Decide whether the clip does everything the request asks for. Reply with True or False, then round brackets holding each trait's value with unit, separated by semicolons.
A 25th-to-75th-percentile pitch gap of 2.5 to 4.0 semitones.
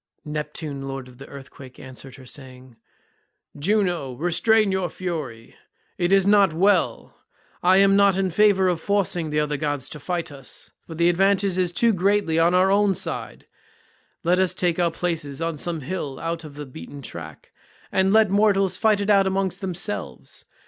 False (5.2 semitones)